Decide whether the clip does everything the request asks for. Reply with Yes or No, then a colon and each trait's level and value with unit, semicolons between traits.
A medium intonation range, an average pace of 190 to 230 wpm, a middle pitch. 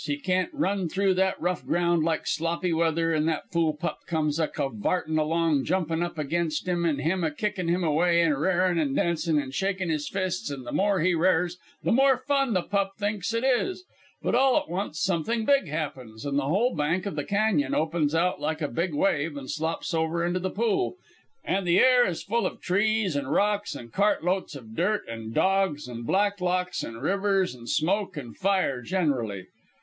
Yes: average, 4.2 semitones; average, 200 wpm; medium, 170 Hz